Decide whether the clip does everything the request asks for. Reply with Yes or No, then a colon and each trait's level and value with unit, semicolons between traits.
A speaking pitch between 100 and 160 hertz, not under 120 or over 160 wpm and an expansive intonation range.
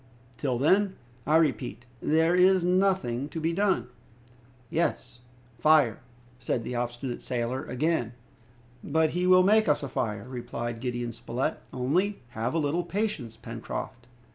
Yes: medium, 140 Hz; average, 140 wpm; wide, 6.3 semitones